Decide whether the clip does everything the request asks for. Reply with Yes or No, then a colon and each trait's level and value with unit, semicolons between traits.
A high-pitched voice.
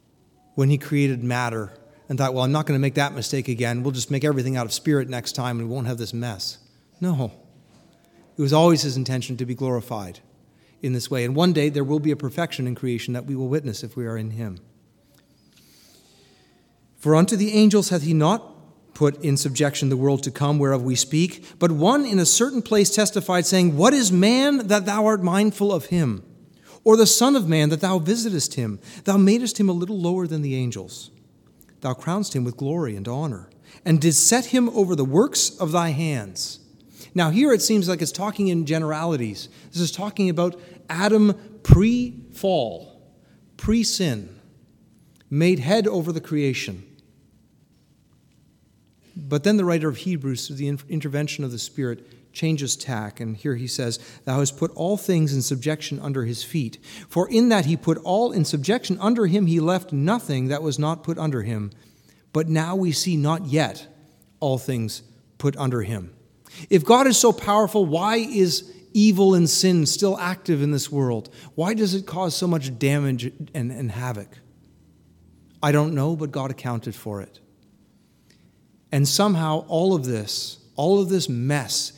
No: medium, 150 Hz